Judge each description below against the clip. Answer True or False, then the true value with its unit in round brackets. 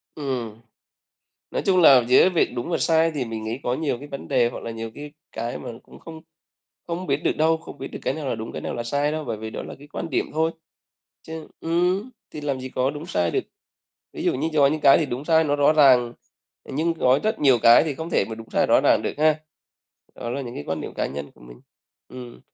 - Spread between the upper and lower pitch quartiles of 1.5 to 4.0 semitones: False (4.9 semitones)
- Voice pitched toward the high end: False (140 Hz)